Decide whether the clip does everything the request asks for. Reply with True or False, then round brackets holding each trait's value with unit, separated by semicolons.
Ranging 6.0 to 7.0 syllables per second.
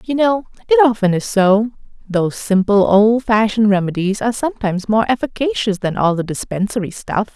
False (5.5 syllables/s)